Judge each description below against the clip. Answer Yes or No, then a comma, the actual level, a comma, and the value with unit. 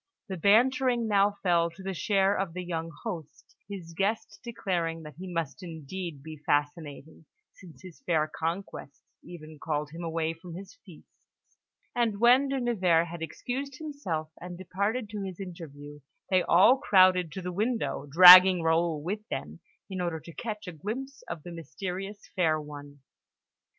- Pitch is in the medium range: Yes, medium, 180 Hz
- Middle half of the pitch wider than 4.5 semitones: No, average, 3.8 semitones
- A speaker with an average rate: Yes, average, 160 wpm